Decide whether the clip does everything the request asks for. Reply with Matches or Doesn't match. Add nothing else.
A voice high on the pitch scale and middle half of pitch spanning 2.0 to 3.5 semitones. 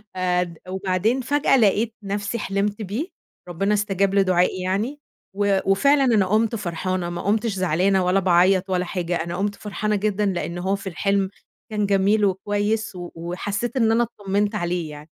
Matches